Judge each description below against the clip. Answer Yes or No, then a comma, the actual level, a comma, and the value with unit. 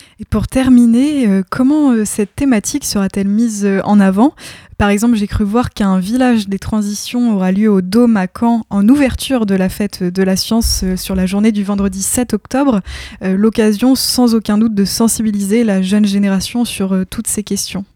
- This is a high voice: Yes, high, 210 Hz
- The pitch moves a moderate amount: Yes, average, 3.3 semitones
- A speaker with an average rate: Yes, average, 195 wpm